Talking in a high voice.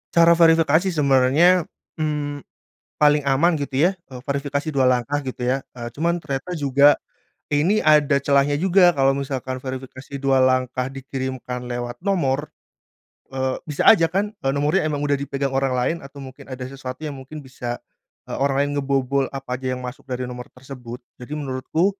No: medium, 140 Hz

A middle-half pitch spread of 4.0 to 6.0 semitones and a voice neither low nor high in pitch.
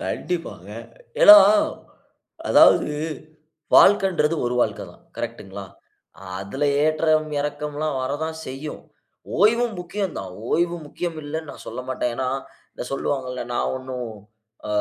Yes: average, 4.7 semitones; medium, 150 Hz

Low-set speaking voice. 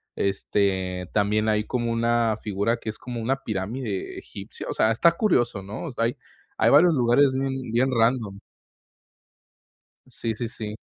Yes: low, 115 Hz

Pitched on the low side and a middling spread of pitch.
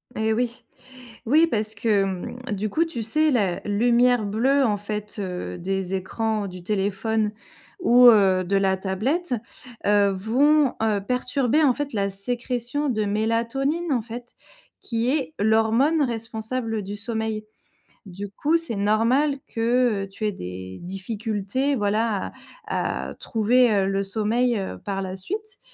No: high, 220 Hz; average, 3.8 semitones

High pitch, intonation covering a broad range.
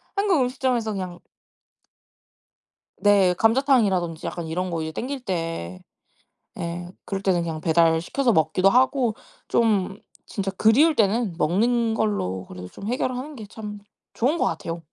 Yes: high, 200 Hz; wide, 6.1 semitones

